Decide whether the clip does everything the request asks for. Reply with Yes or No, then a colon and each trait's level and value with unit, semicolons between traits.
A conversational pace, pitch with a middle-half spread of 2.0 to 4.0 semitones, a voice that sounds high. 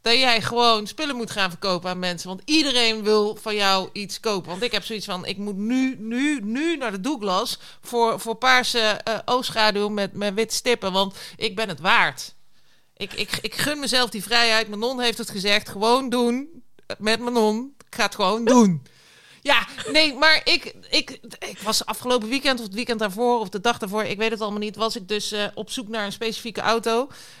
No: fast, 215 wpm; average, 2.8 semitones; high, 225 Hz